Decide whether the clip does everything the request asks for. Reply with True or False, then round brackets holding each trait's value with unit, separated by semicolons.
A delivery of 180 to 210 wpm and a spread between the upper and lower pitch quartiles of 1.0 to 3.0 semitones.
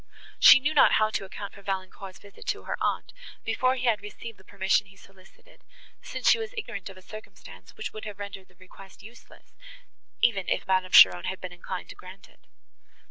True (200 wpm; 2.4 semitones)